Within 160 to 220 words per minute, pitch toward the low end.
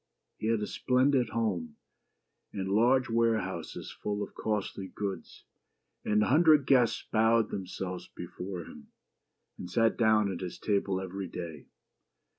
No: average, 140 wpm; low, 105 Hz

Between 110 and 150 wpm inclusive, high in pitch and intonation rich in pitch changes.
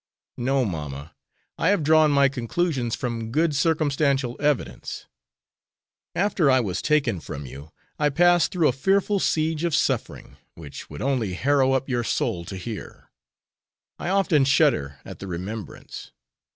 No: average, 145 wpm; low, 135 Hz; wide, 6.1 semitones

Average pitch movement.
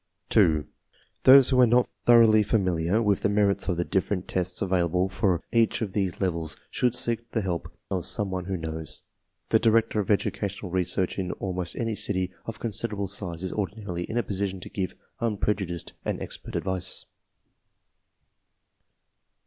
Yes: average, 3.2 semitones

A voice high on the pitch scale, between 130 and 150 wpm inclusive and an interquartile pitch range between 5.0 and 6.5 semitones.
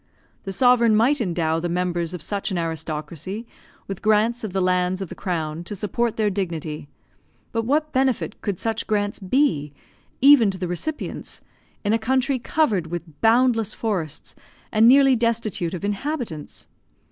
No: high, 205 Hz; average, 160 wpm; average, 5.3 semitones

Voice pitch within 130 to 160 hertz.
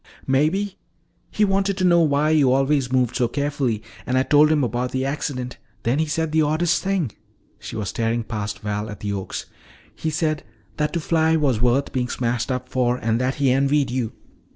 Yes: low, 135 Hz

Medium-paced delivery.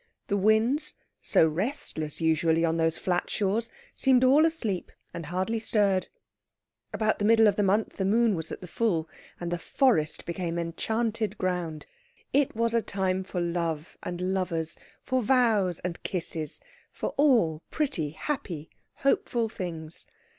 Yes: average, 150 wpm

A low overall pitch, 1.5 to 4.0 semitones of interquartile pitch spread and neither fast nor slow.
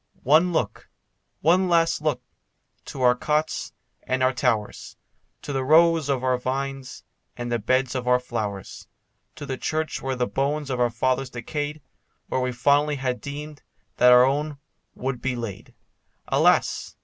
Yes: low, 130 Hz; average, 3.1 semitones; average, 160 wpm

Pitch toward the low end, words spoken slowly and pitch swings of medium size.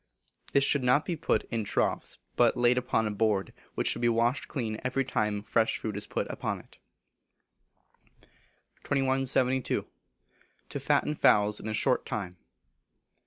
No: low, 120 Hz; average, 150 wpm; average, 3.6 semitones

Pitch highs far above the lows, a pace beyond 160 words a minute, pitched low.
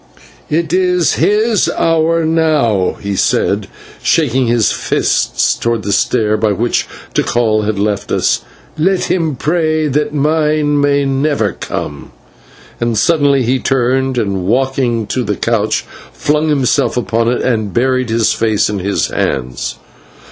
No: wide, 5.8 semitones; average, 140 wpm; low, 130 Hz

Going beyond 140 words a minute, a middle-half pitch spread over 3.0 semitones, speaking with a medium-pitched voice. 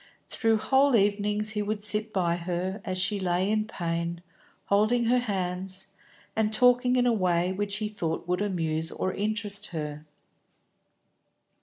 No: average, 150 wpm; average, 3.4 semitones; high, 200 Hz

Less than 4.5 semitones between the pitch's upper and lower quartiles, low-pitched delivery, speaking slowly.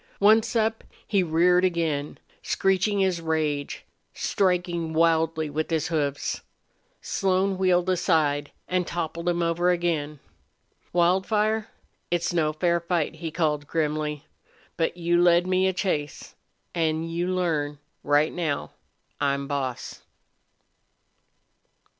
No: average, 2.9 semitones; medium, 170 Hz; slow, 115 wpm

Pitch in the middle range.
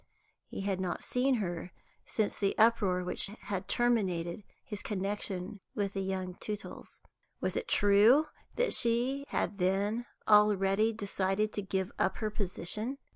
No: high, 200 Hz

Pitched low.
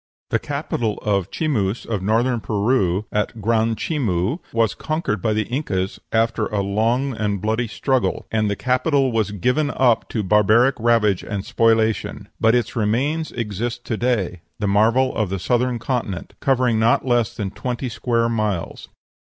Yes: low, 115 Hz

